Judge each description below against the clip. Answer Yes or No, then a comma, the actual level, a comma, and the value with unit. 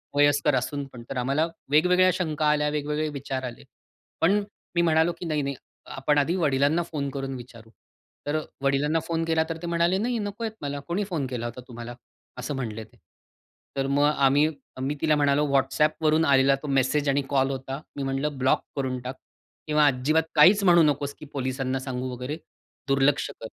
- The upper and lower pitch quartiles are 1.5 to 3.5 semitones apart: Yes, average, 2.9 semitones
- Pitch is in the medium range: Yes, medium, 145 Hz